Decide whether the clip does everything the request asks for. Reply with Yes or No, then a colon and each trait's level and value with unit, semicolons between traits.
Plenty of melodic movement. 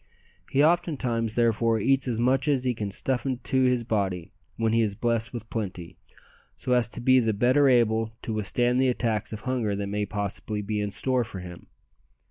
No: average, 3.4 semitones